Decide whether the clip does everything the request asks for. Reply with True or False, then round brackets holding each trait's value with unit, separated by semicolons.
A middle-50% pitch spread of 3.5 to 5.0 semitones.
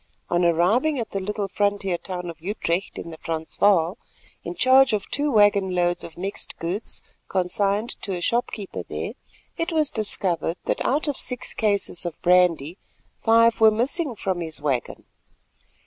True (4.5 semitones)